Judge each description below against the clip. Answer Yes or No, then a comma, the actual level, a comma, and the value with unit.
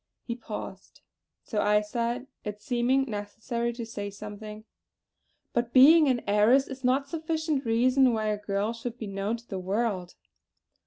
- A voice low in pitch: No, high, 230 Hz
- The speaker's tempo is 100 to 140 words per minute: No, average, 155 wpm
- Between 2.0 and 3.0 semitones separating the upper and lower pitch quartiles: No, average, 3.4 semitones